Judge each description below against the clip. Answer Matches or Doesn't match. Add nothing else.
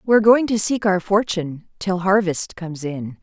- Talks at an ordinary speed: Matches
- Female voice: Matches